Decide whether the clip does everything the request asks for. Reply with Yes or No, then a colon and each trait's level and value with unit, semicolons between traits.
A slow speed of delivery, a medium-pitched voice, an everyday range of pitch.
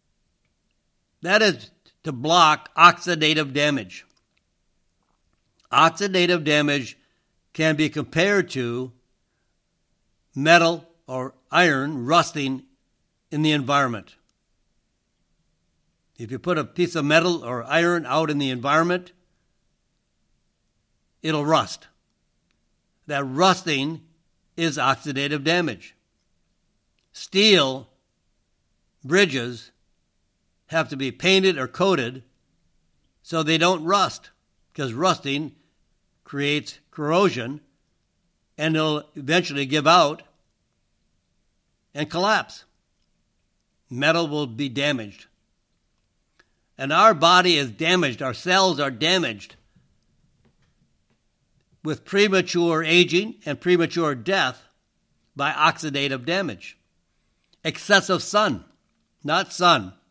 Yes: slow, 90 wpm; medium, 150 Hz; average, 4.7 semitones